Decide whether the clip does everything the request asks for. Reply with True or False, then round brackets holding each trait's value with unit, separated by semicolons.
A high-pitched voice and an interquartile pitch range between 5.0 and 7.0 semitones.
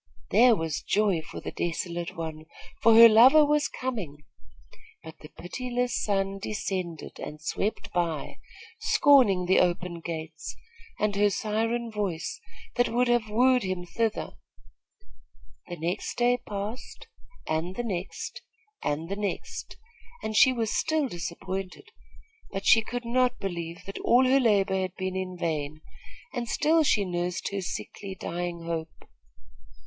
True (195 Hz; 5.3 semitones)